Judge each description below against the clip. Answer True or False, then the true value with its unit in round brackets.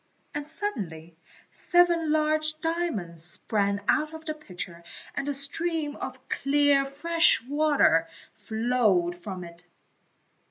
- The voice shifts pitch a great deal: True (8.3 semitones)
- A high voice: True (275 Hz)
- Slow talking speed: True (115 wpm)